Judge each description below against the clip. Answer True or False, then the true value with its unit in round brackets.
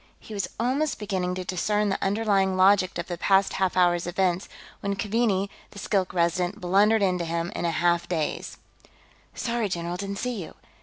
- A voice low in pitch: False (190 Hz)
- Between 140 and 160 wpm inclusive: False (175 wpm)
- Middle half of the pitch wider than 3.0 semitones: False (2.7 semitones)